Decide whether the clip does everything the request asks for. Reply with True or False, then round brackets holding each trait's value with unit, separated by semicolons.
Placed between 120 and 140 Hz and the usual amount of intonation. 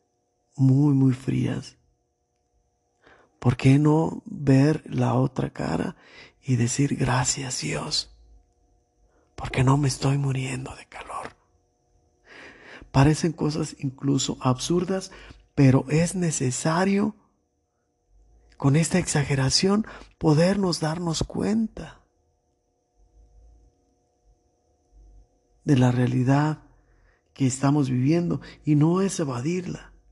True (135 Hz; 4.1 semitones)